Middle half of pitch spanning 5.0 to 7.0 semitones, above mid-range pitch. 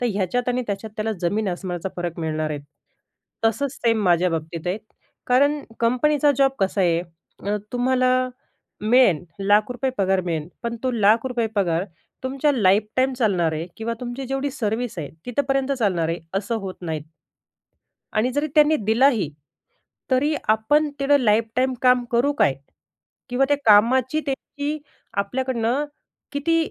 Yes: average, 5.3 semitones; high, 230 Hz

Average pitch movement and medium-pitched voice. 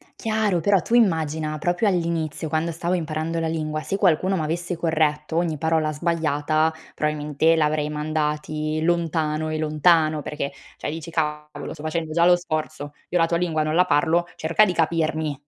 No: narrow, 1.8 semitones; medium, 160 Hz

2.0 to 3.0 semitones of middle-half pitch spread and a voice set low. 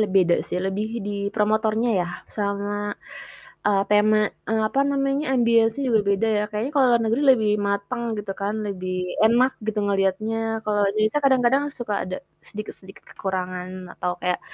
No: average, 2.7 semitones; high, 215 Hz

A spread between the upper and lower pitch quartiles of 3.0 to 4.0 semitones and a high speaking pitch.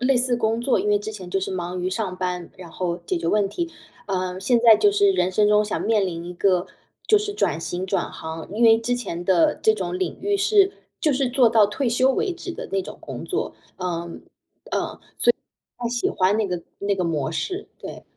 No: average, 5.3 semitones; high, 205 Hz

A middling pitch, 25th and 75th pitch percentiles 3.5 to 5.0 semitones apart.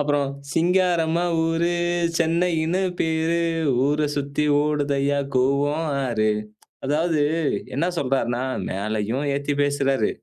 No: medium, 145 Hz; average, 3.1 semitones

